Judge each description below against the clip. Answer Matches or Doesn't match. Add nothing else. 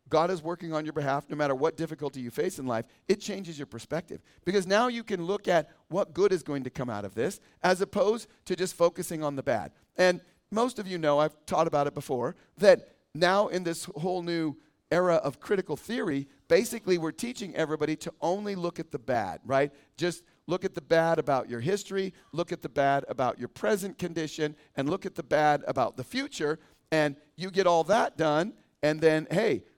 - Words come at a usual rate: Doesn't match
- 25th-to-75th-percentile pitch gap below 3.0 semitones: Doesn't match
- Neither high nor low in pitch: Matches